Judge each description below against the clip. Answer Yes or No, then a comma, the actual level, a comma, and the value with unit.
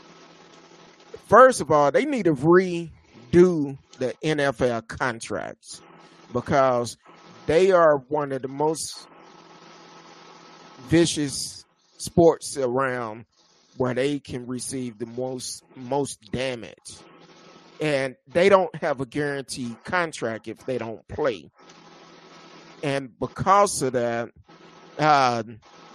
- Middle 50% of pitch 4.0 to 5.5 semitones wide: Yes, average, 4.8 semitones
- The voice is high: No, medium, 140 Hz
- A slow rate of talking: Yes, slow, 100 wpm